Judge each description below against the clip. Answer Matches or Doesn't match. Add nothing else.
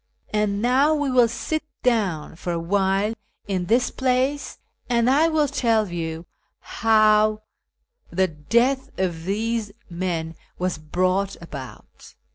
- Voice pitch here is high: Matches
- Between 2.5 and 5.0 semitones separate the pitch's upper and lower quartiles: Doesn't match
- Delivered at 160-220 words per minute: Doesn't match